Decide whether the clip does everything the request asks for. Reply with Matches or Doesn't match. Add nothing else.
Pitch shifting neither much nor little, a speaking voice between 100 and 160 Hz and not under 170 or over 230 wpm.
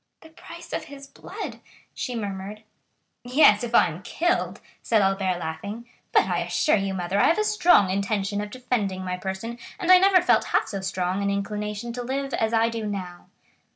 Doesn't match